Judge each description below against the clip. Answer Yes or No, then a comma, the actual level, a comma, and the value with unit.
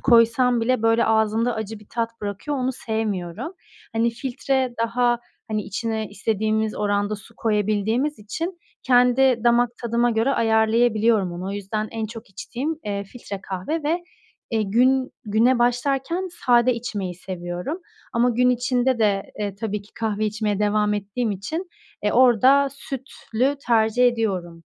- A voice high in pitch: Yes, high, 225 Hz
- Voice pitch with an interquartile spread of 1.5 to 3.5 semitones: Yes, average, 3.0 semitones